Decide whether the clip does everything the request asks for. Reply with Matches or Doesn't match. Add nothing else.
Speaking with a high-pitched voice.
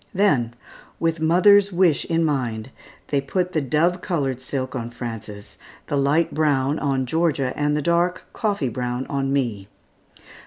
Doesn't match